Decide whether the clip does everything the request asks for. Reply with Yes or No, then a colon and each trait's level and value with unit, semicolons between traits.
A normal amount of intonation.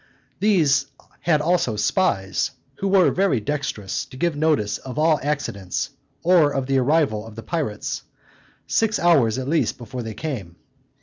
No: wide, 6.6 semitones